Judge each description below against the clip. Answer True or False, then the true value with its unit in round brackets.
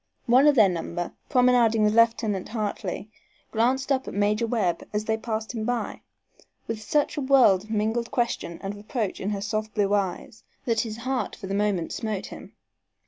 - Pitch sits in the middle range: False (220 Hz)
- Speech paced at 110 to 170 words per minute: False (185 wpm)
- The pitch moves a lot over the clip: False (2.7 semitones)